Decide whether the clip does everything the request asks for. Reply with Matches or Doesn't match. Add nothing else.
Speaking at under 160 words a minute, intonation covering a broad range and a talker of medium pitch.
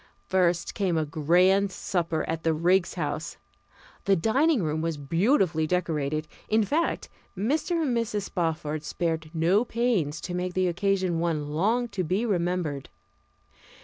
Doesn't match